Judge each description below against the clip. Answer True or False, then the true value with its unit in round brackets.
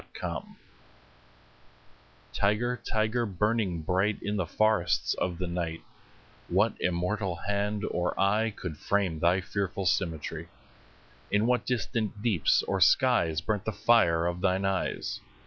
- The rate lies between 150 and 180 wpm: False (135 wpm)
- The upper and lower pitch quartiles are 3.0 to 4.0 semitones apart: True (3.6 semitones)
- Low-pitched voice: True (100 Hz)